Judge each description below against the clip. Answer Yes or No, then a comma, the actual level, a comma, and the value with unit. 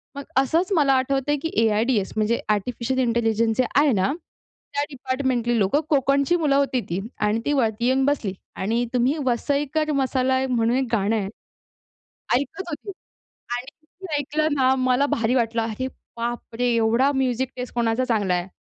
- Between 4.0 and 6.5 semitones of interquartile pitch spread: No, average, 3.4 semitones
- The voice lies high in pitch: Yes, very high, 255 Hz